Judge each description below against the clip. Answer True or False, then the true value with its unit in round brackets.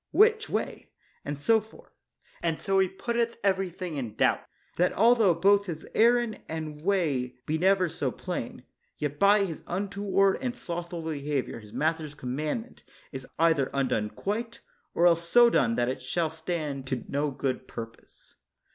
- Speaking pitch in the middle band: True (170 Hz)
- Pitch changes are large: True (5.7 semitones)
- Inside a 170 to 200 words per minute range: False (160 wpm)